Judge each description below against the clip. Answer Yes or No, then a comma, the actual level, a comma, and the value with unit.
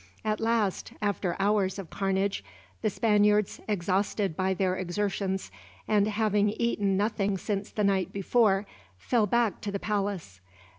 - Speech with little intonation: Yes, narrow, 1.6 semitones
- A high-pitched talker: Yes, high, 200 Hz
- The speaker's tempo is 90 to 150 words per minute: Yes, average, 140 wpm